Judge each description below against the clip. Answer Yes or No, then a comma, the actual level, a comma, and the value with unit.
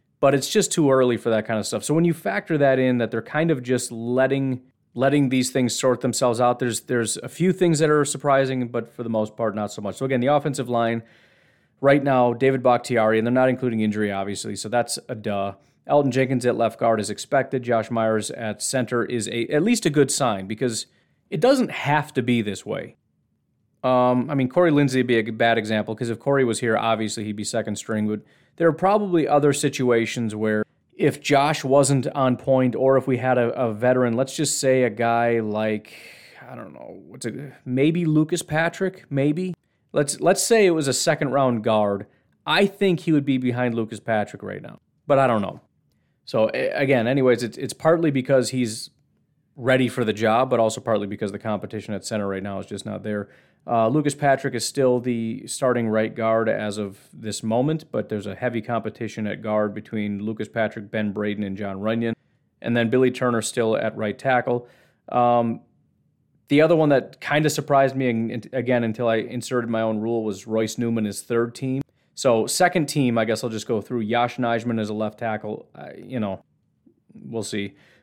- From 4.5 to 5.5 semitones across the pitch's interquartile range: No, average, 3.6 semitones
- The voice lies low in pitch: Yes, low, 120 Hz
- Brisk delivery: Yes, fast, 210 wpm